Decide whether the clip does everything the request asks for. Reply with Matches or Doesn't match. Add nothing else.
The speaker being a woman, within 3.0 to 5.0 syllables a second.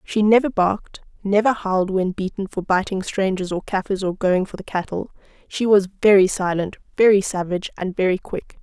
Doesn't match